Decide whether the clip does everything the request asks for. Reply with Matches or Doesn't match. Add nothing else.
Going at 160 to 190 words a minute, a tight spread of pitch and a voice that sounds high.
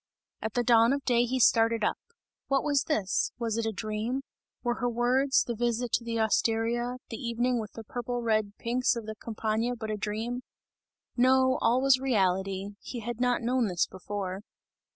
Matches